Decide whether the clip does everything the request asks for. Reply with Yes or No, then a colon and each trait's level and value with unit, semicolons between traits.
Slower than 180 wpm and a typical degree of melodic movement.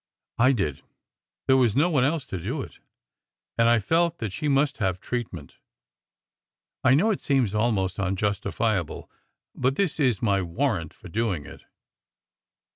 No: average, 155 wpm; wide, 6.0 semitones